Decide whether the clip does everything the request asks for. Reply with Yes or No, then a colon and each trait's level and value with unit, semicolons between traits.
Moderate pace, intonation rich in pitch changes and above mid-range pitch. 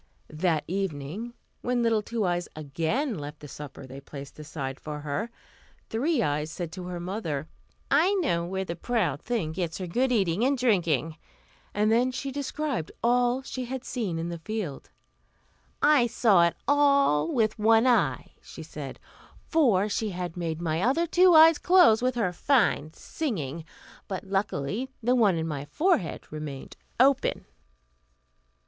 Yes: average, 155 wpm; wide, 7.6 semitones; high, 195 Hz